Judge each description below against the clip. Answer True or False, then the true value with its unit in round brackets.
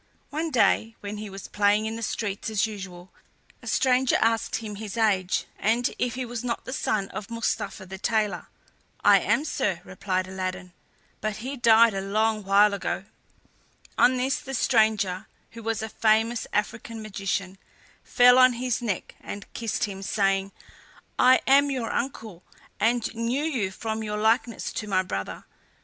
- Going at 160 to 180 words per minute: True (165 wpm)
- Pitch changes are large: False (3.0 semitones)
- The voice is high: True (220 Hz)